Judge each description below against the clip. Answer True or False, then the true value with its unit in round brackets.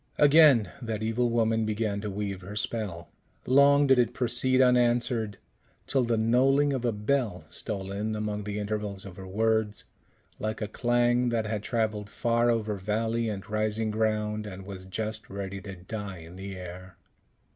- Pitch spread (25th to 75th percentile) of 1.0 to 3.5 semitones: True (2.8 semitones)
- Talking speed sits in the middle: True (165 wpm)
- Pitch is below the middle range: True (110 Hz)